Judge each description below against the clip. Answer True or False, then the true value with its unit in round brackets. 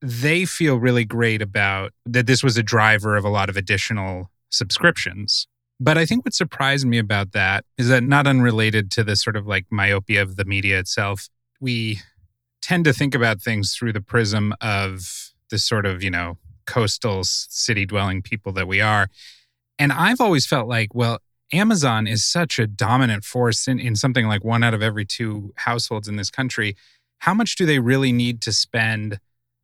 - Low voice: True (115 Hz)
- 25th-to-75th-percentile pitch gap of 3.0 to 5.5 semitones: True (3.5 semitones)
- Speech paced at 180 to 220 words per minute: True (190 wpm)